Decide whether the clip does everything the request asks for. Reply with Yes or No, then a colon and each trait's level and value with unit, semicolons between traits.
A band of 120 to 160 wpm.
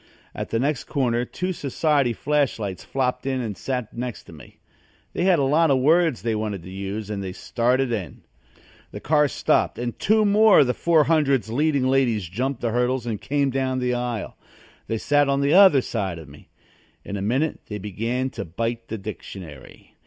No: average, 195 wpm